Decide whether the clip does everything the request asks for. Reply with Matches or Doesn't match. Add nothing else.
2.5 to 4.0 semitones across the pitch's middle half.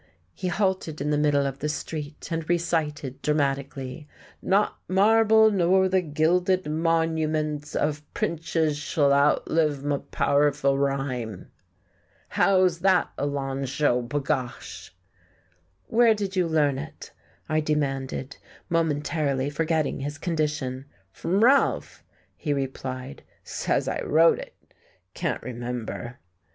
Matches